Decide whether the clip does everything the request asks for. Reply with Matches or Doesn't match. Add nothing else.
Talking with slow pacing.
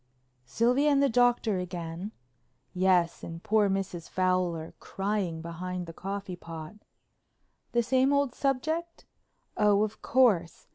Matches